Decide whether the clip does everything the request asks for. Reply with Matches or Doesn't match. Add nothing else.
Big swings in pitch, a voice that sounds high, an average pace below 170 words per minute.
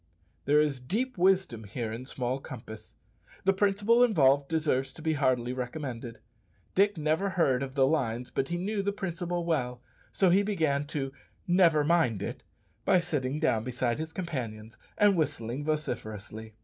Doesn't match